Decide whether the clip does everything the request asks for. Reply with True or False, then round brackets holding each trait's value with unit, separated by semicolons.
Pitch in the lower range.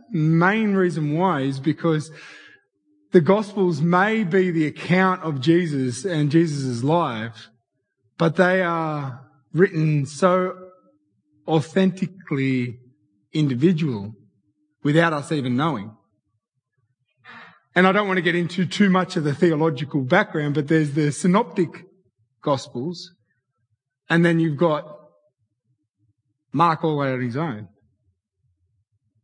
False (155 Hz)